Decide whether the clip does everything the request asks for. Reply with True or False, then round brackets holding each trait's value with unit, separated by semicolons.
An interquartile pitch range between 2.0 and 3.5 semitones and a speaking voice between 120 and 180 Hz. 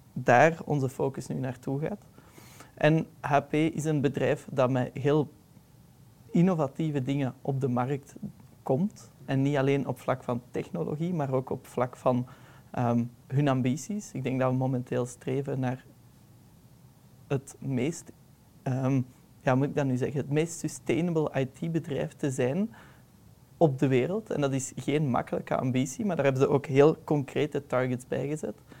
True (2.9 semitones; 135 Hz)